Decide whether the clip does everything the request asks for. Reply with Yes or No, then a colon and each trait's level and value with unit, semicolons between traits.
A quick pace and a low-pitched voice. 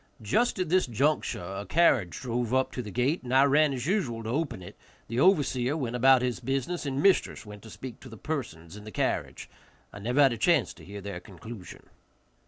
Yes: fast, 215 wpm; low, 125 Hz